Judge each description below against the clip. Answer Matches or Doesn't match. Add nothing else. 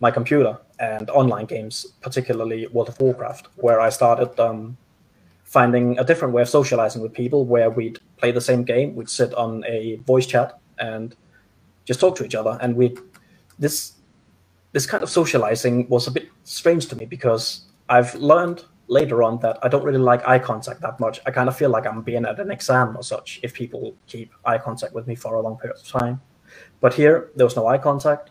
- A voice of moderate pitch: Doesn't match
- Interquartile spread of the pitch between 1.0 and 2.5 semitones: Doesn't match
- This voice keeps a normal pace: Doesn't match